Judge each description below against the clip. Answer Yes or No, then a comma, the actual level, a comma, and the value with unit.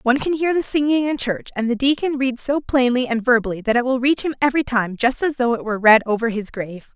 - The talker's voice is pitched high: Yes, very high, 250 Hz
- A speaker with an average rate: No, fast, 265 wpm